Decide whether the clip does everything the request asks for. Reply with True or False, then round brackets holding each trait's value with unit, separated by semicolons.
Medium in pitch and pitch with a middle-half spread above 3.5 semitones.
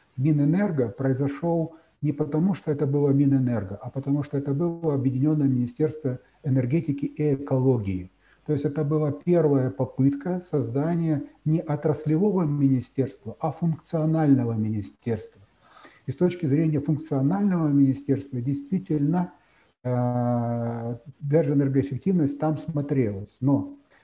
False (145 Hz; 2.9 semitones)